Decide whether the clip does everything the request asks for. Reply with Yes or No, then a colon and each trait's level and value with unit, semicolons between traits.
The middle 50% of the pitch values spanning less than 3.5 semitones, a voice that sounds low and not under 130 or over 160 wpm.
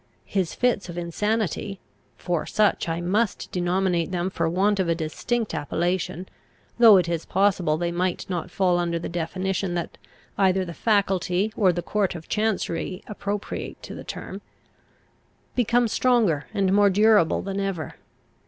No: average, 3.0 semitones; medium, 185 Hz; average, 155 wpm